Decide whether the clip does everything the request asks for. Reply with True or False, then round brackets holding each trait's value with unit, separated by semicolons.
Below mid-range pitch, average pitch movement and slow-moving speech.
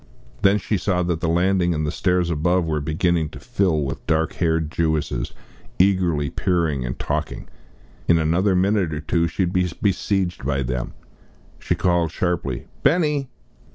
False (85 Hz; 3.0 semitones; 160 wpm)